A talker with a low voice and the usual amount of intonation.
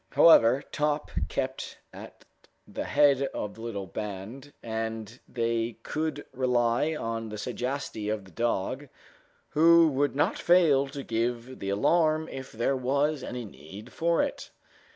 Yes: low, 125 Hz; average, 4.4 semitones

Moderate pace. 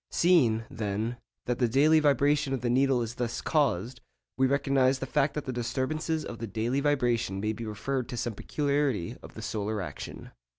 Yes: average, 185 wpm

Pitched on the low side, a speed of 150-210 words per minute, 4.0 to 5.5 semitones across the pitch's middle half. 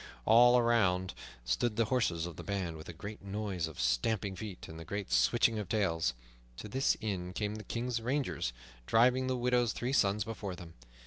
Yes: low, 105 Hz; average, 190 wpm; average, 4.9 semitones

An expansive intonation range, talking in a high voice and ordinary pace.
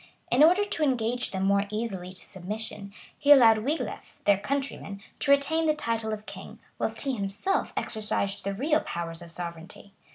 Yes: wide, 6.0 semitones; high, 220 Hz; average, 170 wpm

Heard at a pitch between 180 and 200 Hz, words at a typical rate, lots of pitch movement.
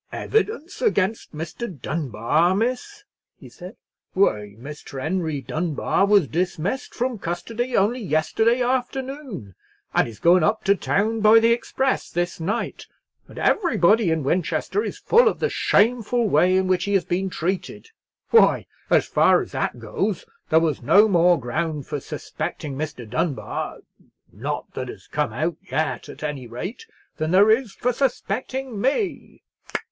Yes: high, 190 Hz; average, 145 wpm; wide, 7.4 semitones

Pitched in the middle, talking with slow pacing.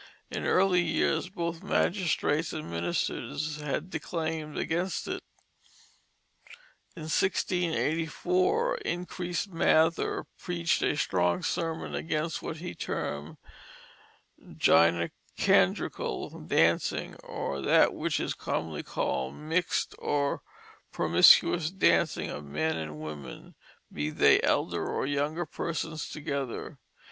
Yes: medium, 155 Hz; slow, 100 wpm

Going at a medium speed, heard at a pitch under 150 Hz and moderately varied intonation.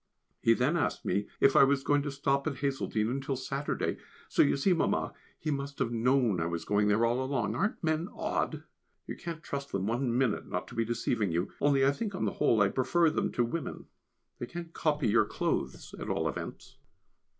No: fast, 210 wpm; low, 135 Hz; average, 3.9 semitones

